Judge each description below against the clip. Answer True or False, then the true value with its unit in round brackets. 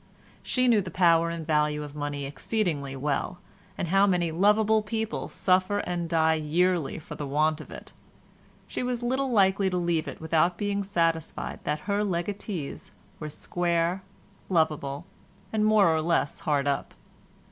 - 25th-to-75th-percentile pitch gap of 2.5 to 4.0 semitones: False (4.6 semitones)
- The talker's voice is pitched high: False (170 Hz)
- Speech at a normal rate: True (160 wpm)